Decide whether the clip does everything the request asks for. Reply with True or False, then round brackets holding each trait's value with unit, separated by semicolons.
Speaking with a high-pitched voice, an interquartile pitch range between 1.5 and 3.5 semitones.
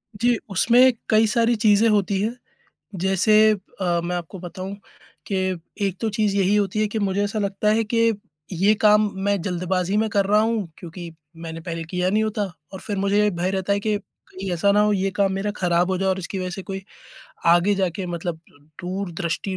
True (195 Hz; 2.5 semitones)